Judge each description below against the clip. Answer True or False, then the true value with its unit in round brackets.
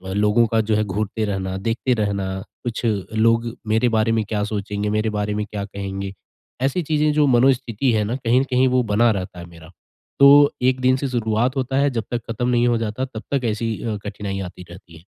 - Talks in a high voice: False (110 Hz)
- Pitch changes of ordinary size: True (3.4 semitones)